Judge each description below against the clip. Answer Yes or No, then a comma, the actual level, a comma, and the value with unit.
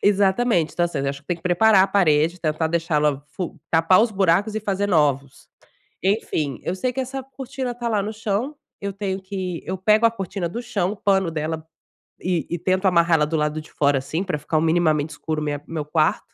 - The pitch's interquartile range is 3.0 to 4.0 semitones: No, average, 4.5 semitones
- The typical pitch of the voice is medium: Yes, medium, 180 Hz